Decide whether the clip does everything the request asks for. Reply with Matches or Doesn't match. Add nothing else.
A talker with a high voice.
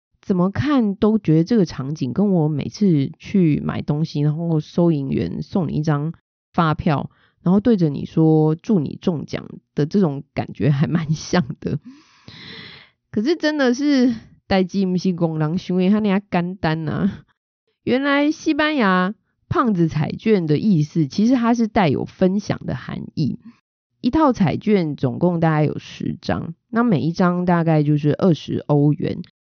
Doesn't match